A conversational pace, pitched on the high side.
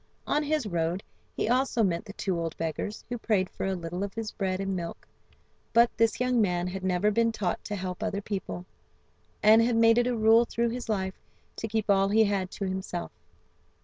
No: fast, 210 wpm; high, 205 Hz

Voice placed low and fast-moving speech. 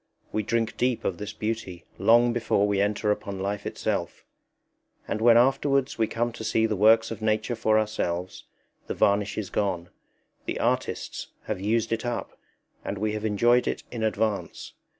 No: low, 110 Hz; average, 170 wpm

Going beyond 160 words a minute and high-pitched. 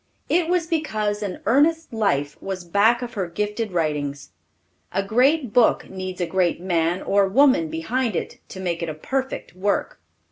Yes: average, 170 wpm; high, 200 Hz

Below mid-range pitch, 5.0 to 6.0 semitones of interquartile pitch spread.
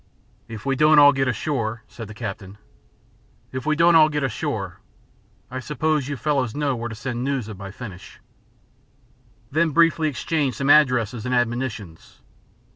No: low, 130 Hz; average, 4.5 semitones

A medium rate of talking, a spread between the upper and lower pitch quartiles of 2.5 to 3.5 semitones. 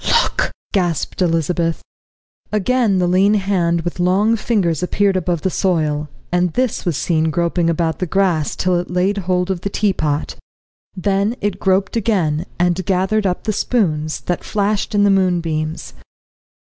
Yes: average, 155 wpm; average, 2.9 semitones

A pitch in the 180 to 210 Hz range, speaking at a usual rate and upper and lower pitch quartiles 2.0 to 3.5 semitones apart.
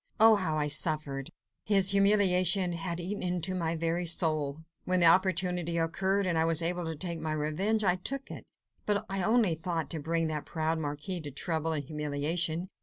No: medium, 170 Hz; average, 185 wpm; average, 2.9 semitones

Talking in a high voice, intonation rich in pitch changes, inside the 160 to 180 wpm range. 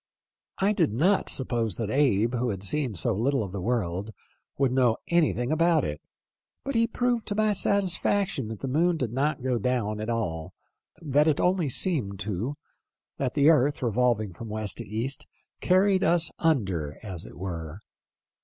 No: low, 125 Hz; wide, 7.2 semitones; average, 175 wpm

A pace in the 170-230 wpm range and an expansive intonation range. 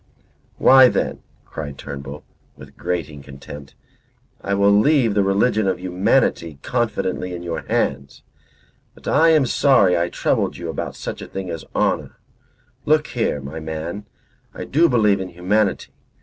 No: average, 150 wpm; wide, 6.1 semitones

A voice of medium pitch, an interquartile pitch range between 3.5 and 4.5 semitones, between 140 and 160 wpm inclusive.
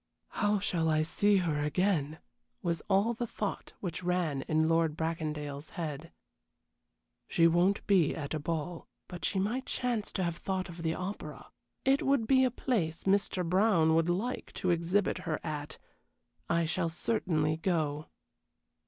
Yes: medium, 170 Hz; average, 3.9 semitones; average, 155 wpm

